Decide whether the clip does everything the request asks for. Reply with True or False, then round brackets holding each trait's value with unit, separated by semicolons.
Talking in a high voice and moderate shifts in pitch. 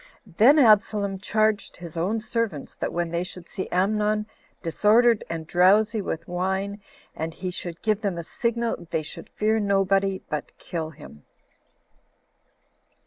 True (195 Hz; 3.8 semitones)